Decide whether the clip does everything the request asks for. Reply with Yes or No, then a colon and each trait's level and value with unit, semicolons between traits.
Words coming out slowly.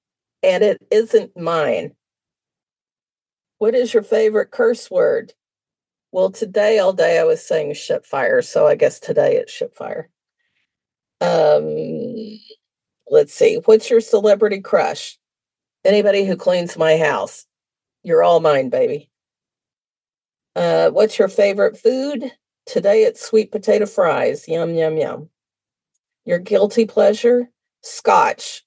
Yes: slow, 120 wpm